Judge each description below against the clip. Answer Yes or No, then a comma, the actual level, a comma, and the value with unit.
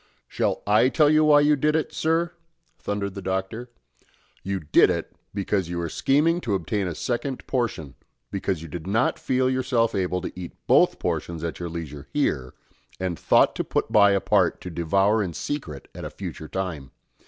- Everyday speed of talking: Yes, average, 190 wpm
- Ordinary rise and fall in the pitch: No, wide, 6.9 semitones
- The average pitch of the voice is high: No, low, 100 Hz